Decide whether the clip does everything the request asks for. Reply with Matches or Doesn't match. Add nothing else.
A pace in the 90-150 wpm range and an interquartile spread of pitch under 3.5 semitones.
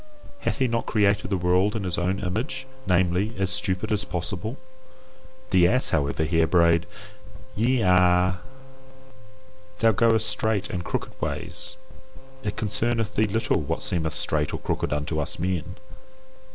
Doesn't match